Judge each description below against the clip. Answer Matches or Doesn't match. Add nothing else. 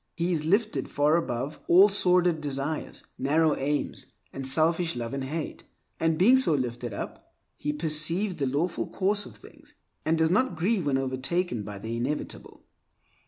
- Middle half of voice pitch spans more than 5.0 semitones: Doesn't match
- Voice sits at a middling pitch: Matches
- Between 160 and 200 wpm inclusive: Matches